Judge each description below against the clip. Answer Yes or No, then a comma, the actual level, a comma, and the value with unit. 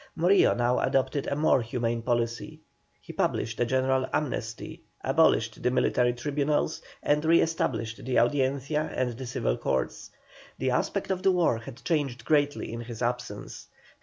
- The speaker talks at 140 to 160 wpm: Yes, average, 155 wpm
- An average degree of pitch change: Yes, average, 3.8 semitones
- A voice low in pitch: Yes, low, 130 Hz